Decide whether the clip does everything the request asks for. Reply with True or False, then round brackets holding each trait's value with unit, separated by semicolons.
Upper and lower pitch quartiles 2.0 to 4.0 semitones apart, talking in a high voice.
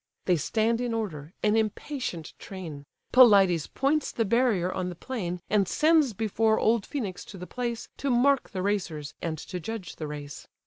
False (5.1 semitones; 205 Hz)